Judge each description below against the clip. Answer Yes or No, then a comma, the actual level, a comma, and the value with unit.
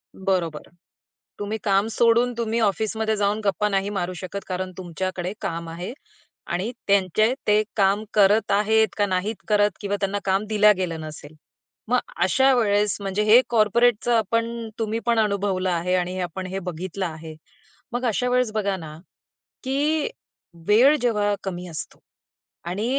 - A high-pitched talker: Yes, high, 205 Hz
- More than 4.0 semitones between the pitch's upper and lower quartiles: No, average, 3.0 semitones